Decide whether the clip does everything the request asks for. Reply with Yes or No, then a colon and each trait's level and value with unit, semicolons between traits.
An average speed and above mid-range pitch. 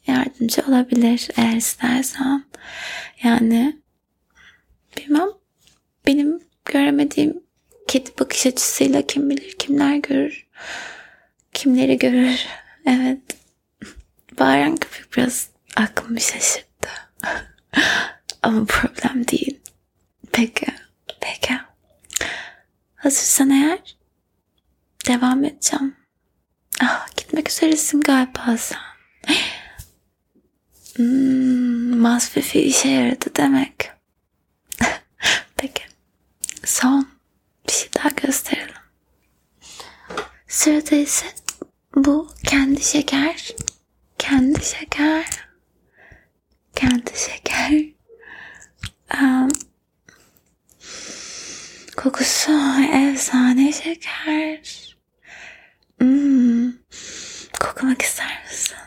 No: slow, 65 wpm; very high, 275 Hz